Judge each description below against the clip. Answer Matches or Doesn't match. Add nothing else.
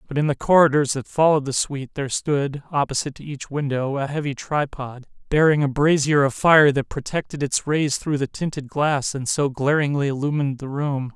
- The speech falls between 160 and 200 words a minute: Matches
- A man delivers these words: Matches